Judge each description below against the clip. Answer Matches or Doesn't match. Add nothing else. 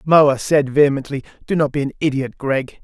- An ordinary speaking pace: Matches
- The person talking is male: Matches